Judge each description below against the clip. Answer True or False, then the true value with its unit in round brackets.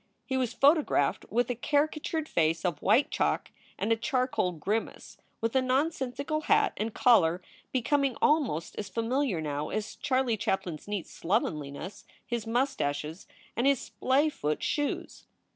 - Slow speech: False (145 wpm)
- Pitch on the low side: False (235 Hz)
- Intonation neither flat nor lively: False (7.3 semitones)